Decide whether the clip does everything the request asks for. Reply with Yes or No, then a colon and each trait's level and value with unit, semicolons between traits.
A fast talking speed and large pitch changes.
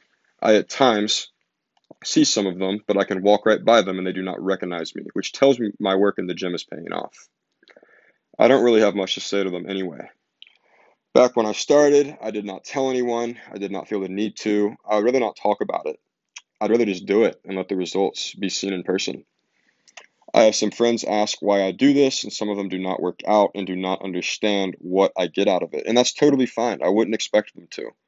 No: fast, 240 wpm; average, 3.6 semitones